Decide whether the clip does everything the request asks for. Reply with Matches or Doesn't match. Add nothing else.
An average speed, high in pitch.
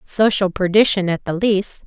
Matches